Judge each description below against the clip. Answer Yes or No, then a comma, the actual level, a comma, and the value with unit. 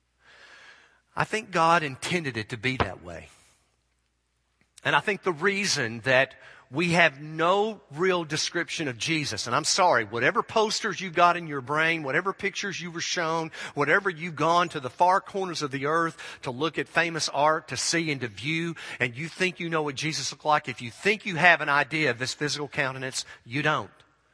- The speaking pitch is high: No, medium, 155 Hz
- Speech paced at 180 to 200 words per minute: Yes, average, 195 wpm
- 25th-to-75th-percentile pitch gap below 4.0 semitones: No, average, 4.7 semitones